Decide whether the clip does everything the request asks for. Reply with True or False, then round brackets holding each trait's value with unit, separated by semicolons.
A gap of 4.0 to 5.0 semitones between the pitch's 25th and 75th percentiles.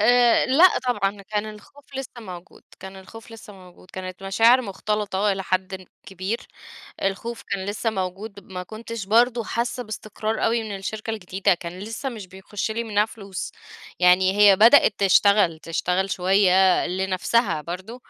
False (3.1 semitones)